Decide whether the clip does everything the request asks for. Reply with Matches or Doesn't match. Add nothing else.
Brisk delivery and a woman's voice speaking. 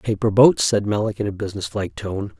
Doesn't match